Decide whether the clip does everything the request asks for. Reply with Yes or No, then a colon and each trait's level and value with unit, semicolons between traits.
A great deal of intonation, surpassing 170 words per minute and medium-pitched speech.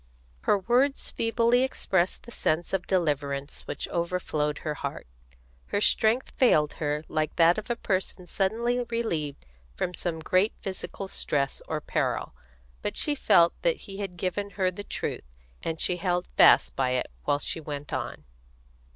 No: wide, 5.8 semitones; average, 160 wpm; medium, 180 Hz